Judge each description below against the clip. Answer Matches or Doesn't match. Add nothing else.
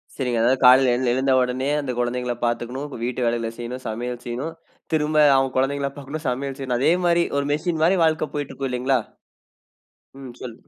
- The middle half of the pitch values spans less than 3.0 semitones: Matches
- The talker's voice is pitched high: Doesn't match